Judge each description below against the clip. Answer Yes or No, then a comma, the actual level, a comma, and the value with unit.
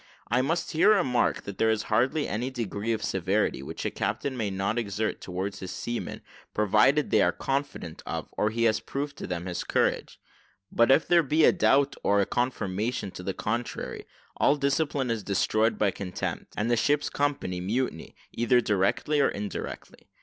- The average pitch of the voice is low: Yes, low, 115 Hz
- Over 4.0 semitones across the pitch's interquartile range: Yes, average, 5.3 semitones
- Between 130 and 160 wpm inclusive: No, average, 180 wpm